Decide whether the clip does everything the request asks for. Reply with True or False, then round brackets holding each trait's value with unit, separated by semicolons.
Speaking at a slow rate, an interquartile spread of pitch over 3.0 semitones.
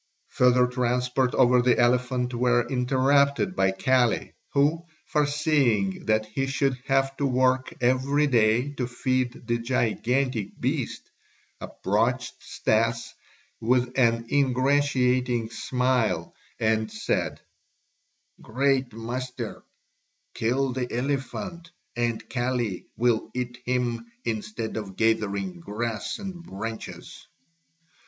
False (105 wpm; 2.5 semitones)